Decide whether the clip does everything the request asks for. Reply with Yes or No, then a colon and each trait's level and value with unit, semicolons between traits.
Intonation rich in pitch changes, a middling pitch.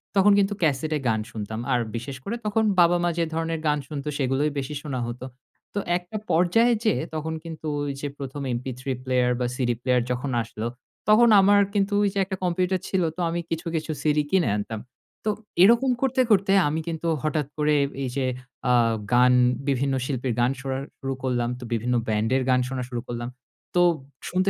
Yes: wide, 5.9 semitones; medium, 150 Hz